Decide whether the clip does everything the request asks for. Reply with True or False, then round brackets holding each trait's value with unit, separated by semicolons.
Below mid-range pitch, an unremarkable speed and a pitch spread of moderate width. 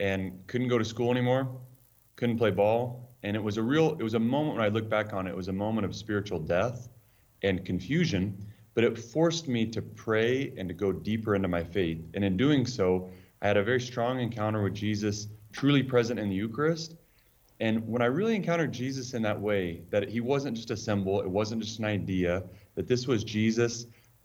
False (110 Hz; 215 wpm; 3.4 semitones)